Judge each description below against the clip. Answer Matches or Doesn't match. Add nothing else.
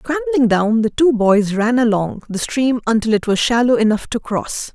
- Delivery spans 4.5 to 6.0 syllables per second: Matches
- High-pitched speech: Matches